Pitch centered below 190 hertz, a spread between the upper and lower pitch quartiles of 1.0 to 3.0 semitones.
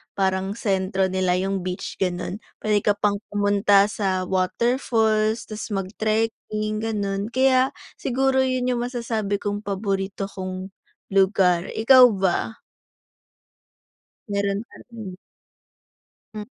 No: high, 205 Hz; narrow, 2.6 semitones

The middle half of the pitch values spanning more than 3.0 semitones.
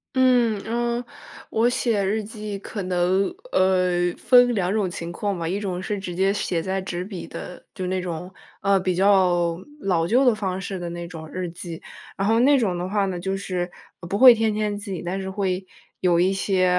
No: average, 2.7 semitones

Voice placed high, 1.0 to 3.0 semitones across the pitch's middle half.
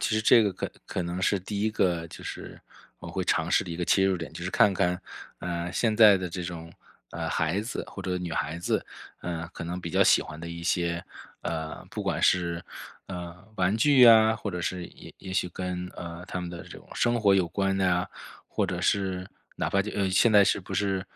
No: very low, 90 Hz; narrow, 2.4 semitones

